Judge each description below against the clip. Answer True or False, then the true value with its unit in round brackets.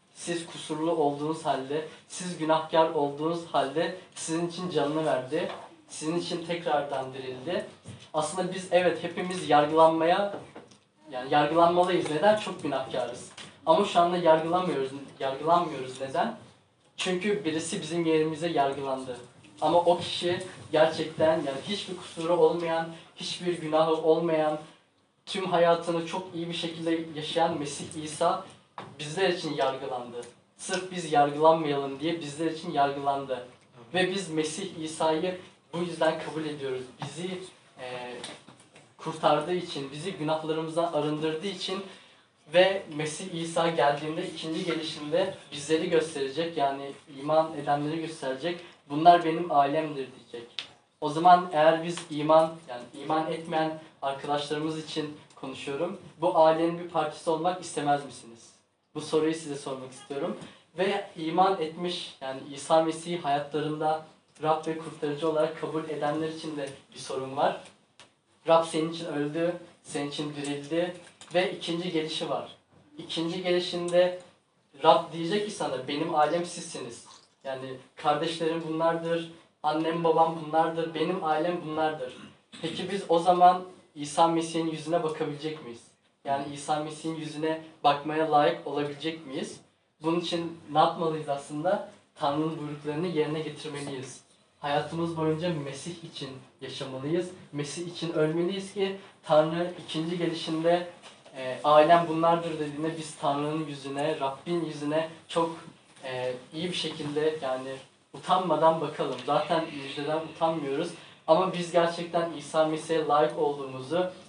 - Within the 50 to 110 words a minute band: False (125 wpm)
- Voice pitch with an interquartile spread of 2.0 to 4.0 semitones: True (2.5 semitones)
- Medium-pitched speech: True (160 Hz)